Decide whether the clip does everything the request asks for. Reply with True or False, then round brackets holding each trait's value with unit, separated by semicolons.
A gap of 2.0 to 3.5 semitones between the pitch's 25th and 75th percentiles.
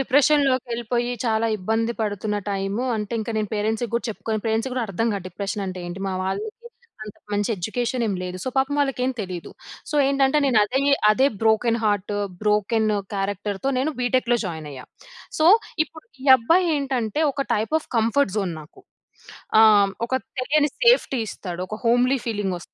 False (4.3 semitones)